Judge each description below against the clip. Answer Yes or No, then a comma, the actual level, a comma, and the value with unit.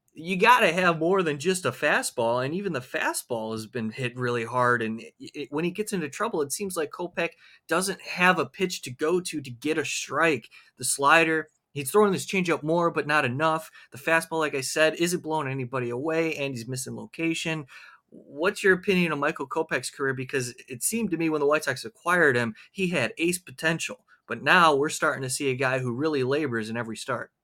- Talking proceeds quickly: Yes, fast, 215 wpm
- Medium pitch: Yes, medium, 155 Hz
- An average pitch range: Yes, average, 4.6 semitones